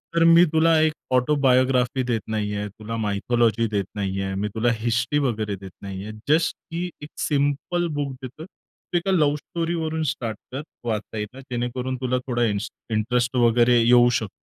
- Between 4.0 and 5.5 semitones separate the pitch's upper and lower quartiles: Yes, average, 4.9 semitones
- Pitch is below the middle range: Yes, low, 125 Hz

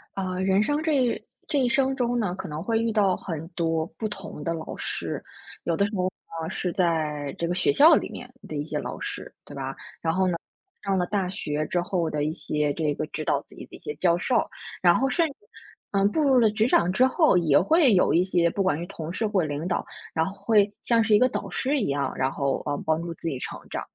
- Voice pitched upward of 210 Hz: No, medium, 185 Hz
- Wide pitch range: Yes, wide, 5.7 semitones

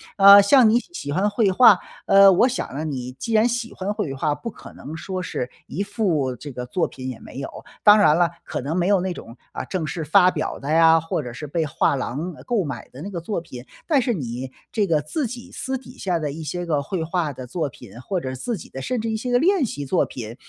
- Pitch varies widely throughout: Yes, wide, 6.6 semitones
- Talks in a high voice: No, medium, 170 Hz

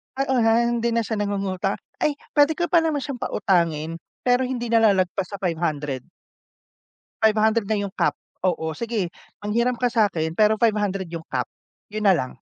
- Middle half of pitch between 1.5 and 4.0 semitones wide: No, average, 4.7 semitones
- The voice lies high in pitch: Yes, high, 215 Hz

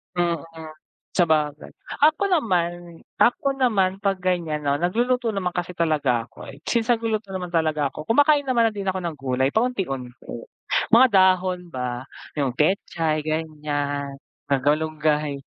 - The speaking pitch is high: No, medium, 175 Hz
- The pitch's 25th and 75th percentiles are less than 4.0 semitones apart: No, average, 5.3 semitones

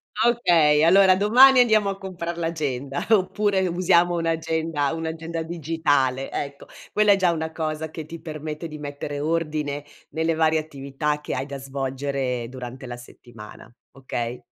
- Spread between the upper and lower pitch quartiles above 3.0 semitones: Yes, average, 3.4 semitones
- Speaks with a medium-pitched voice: Yes, medium, 160 Hz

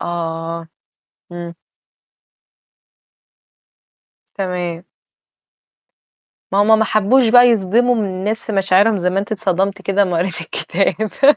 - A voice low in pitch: No, high, 195 Hz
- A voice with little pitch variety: No, average, 3.7 semitones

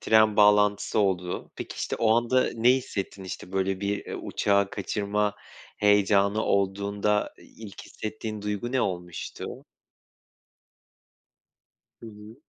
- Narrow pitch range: Yes, narrow, 1.6 semitones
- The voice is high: No, low, 105 Hz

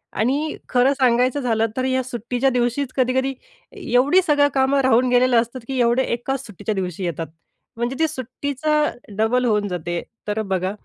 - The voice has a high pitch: Yes, very high, 250 Hz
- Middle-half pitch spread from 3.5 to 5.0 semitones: No, average, 3.0 semitones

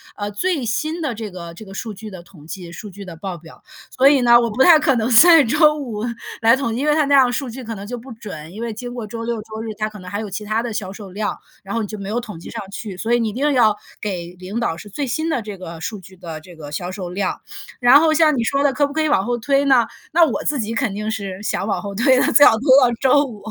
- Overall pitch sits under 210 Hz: No, high, 225 Hz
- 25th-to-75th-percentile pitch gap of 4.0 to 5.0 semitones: Yes, average, 4.6 semitones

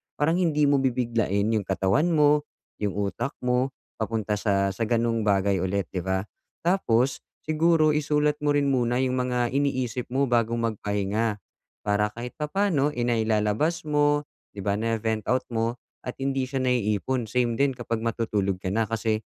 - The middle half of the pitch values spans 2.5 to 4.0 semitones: No, average, 4.6 semitones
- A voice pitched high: No, low, 120 Hz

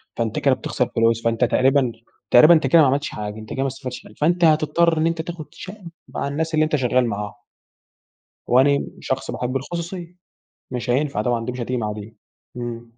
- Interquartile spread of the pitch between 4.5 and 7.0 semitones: Yes, average, 4.9 semitones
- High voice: No, low, 130 Hz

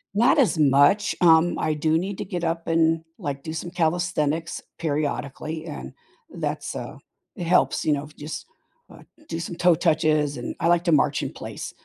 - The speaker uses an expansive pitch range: No, narrow, 2.4 semitones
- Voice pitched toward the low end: No, medium, 160 Hz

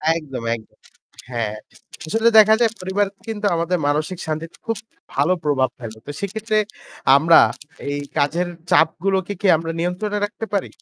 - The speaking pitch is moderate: Yes, medium, 170 Hz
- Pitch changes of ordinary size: No, wide, 5.9 semitones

